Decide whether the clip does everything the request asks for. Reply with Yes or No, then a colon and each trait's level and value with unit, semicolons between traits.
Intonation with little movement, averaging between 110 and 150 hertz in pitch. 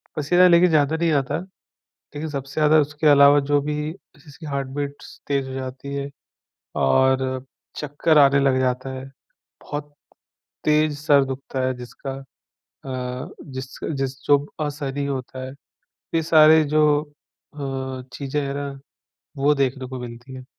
Yes: narrow, 2.0 semitones; medium, 140 Hz